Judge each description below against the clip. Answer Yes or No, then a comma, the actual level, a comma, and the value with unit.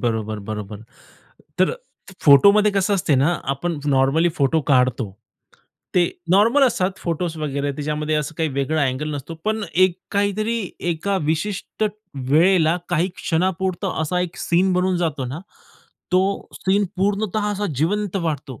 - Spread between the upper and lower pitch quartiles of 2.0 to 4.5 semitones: No, average, 5.1 semitones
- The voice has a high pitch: No, medium, 165 Hz